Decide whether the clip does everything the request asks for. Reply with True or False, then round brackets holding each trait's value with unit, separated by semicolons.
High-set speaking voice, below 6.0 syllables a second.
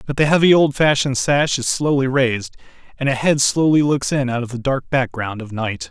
False (135 Hz; 5.4 syllables/s)